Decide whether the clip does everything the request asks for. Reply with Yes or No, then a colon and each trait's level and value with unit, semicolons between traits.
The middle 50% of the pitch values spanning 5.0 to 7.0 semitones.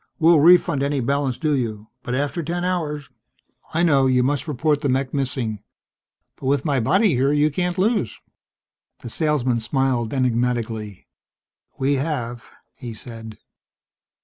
No: average, 3.7 semitones